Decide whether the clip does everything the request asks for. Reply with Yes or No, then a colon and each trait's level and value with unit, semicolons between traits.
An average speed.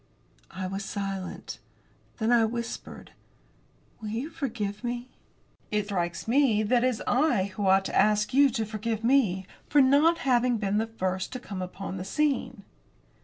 Yes: average, 165 wpm